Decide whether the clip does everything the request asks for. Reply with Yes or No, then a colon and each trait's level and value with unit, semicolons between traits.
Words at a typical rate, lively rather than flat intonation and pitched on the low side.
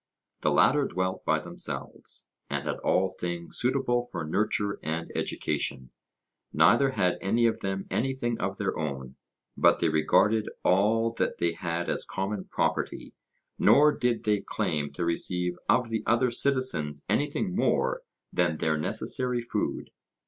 Yes: average, 145 wpm; wide, 6.2 semitones; low, 100 Hz